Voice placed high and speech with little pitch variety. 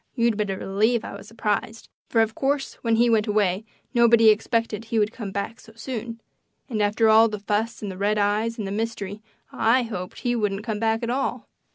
Yes: high, 220 Hz; narrow, 1.8 semitones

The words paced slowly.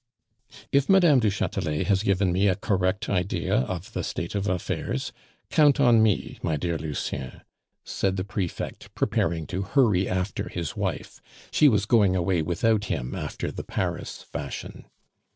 No: average, 155 wpm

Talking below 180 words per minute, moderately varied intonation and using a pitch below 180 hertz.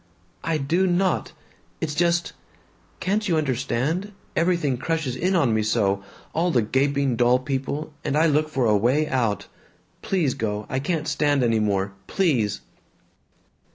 No: average, 150 wpm; wide, 5.7 semitones; medium, 140 Hz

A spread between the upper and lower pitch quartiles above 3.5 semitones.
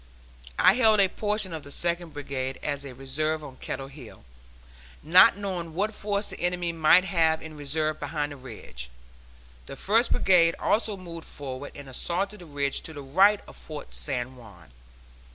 Yes: average, 4.9 semitones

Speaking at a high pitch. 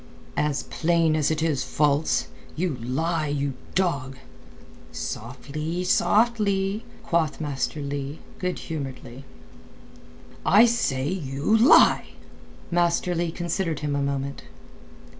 No: medium, 155 Hz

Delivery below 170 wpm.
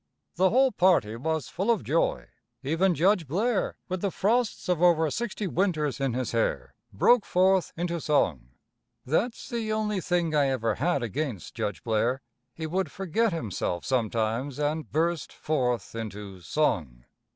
Yes: average, 150 wpm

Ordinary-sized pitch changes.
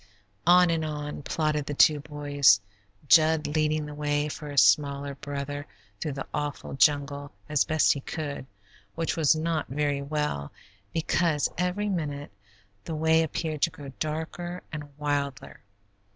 No: narrow, 1.8 semitones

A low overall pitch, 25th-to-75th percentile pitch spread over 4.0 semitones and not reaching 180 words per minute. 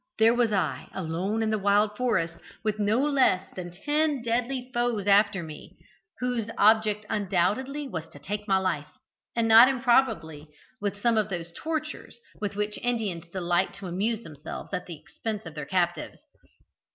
No: high, 210 Hz; average, 4.6 semitones; average, 165 wpm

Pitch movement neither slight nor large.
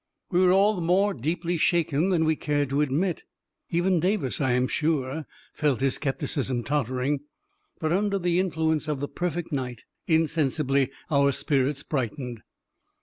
Yes: average, 4.3 semitones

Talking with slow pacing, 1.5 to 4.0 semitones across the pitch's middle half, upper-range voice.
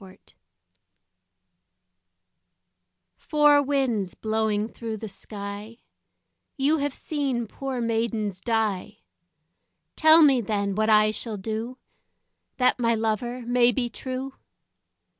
Yes: slow, 105 wpm; average, 3.3 semitones; high, 230 Hz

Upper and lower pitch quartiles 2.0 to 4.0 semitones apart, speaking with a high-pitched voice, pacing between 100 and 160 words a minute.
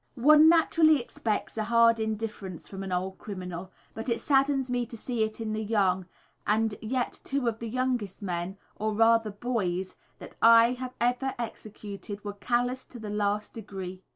No: average, 3.4 semitones; high, 220 Hz; average, 175 wpm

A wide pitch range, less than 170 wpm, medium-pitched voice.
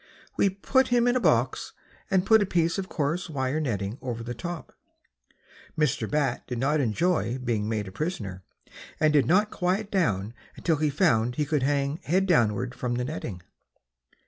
No: wide, 6.7 semitones; average, 175 wpm; medium, 145 Hz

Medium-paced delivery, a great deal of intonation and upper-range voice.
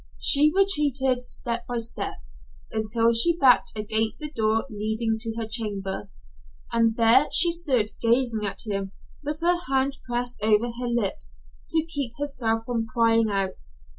No: average, 150 wpm; average, 3.4 semitones; high, 230 Hz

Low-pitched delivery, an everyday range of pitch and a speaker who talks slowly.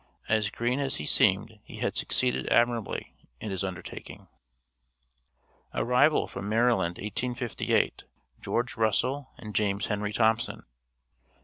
Yes: low, 110 Hz; average, 3.3 semitones; slow, 115 wpm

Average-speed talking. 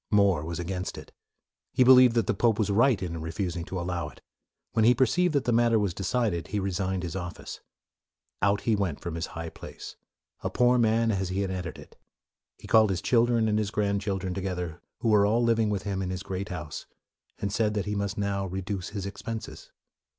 No: fast, 210 wpm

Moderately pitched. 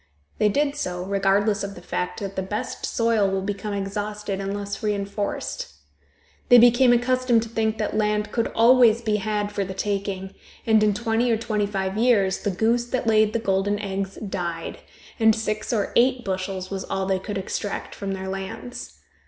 No: high, 205 Hz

